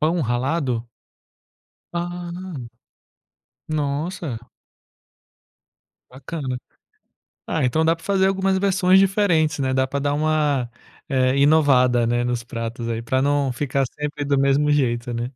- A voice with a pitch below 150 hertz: Yes, medium, 140 Hz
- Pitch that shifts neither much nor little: Yes, average, 4.3 semitones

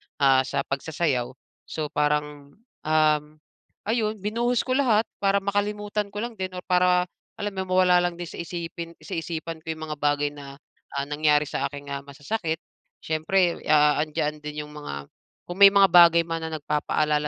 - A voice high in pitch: No, medium, 160 Hz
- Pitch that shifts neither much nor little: Yes, average, 4.1 semitones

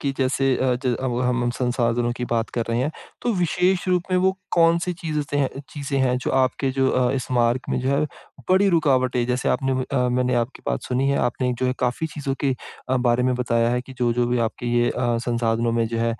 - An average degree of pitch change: No, narrow, 2.3 semitones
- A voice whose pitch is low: Yes, low, 125 Hz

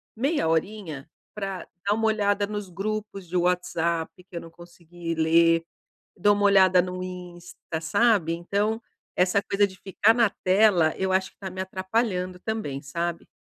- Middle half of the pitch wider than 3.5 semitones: No, average, 3.1 semitones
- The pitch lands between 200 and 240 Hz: No, medium, 185 Hz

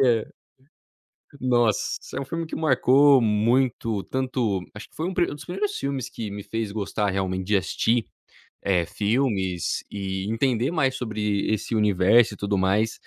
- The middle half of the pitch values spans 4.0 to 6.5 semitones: Yes, average, 4.5 semitones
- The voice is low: Yes, low, 110 Hz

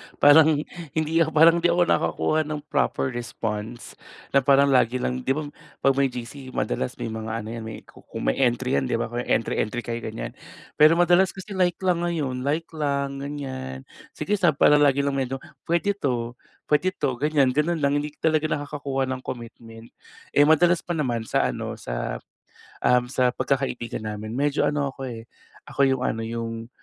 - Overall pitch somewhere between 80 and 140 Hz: Yes, low, 135 Hz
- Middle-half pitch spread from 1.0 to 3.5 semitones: No, average, 4.5 semitones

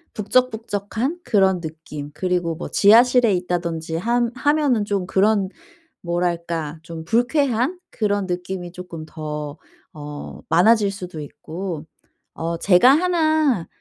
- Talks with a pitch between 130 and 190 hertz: Yes, medium, 185 Hz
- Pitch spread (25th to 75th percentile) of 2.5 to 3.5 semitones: No, wide, 5.5 semitones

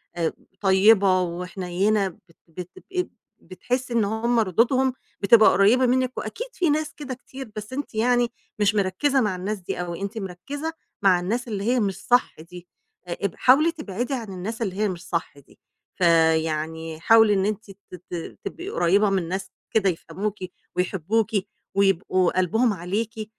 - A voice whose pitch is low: No, high, 200 Hz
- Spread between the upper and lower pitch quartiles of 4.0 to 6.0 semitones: Yes, average, 4.8 semitones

